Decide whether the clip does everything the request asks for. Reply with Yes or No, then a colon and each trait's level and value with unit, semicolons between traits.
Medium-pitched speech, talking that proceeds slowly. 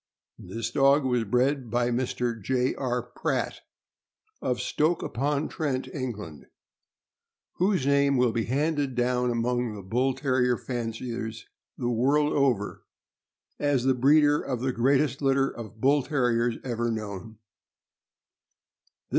No: low, 125 Hz; slow, 125 wpm